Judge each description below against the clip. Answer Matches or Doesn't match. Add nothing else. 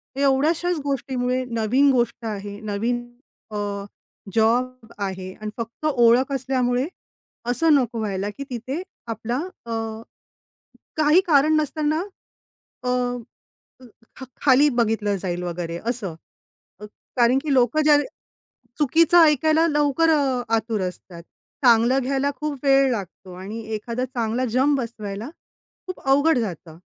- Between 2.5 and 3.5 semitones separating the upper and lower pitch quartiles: Doesn't match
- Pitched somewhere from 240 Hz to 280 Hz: Matches